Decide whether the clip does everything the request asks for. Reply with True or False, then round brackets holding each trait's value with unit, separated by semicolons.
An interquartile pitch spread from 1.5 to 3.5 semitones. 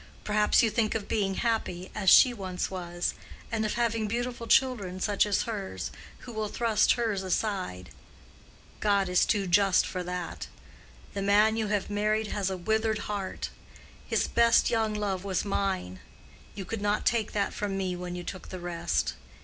True (2.8 semitones)